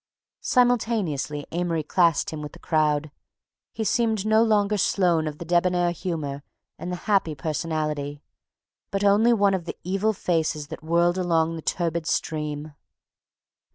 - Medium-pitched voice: Yes, medium, 170 Hz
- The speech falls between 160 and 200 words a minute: No, average, 150 wpm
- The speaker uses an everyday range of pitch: Yes, average, 4.3 semitones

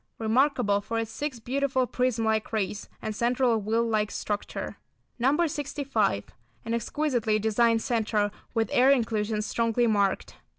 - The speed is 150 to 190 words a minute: No, slow, 135 wpm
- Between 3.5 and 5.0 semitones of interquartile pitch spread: No, average, 2.8 semitones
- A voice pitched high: Yes, high, 230 Hz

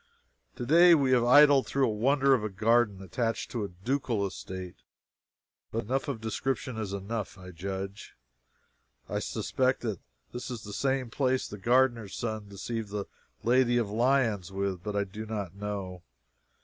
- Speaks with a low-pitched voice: Yes, low, 110 Hz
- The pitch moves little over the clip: No, average, 4.4 semitones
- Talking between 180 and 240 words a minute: No, average, 160 wpm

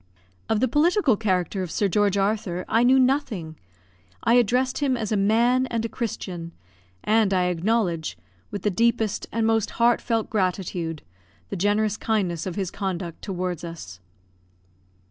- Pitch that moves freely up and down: No, average, 4.2 semitones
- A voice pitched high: Yes, high, 205 Hz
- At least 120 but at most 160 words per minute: Yes, average, 150 wpm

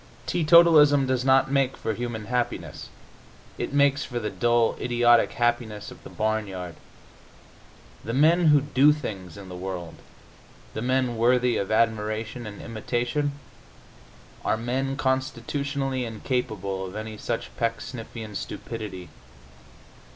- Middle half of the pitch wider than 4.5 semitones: No, average, 3.6 semitones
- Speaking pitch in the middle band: No, low, 120 Hz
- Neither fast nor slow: No, slow, 120 wpm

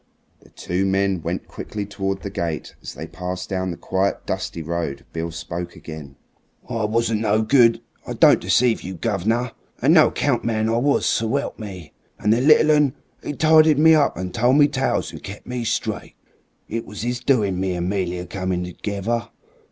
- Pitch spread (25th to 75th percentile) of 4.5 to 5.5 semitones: Yes, average, 4.9 semitones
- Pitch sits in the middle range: No, low, 100 Hz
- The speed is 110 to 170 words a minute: No, average, 185 wpm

